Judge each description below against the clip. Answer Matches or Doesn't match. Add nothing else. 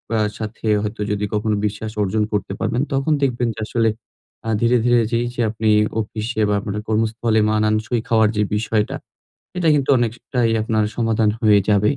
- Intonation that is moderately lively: Doesn't match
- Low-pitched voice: Matches